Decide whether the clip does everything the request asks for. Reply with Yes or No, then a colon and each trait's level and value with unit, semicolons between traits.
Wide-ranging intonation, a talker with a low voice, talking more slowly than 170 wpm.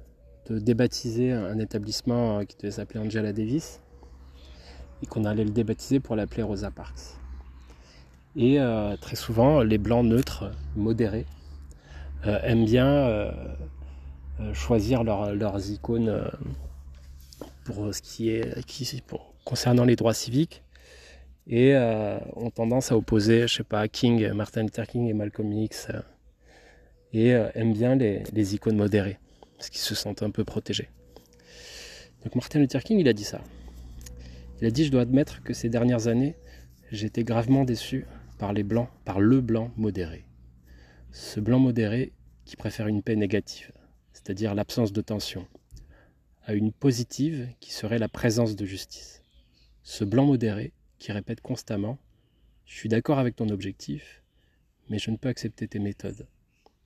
Yes: wide, 7.3 semitones; low, 110 Hz; average, 150 wpm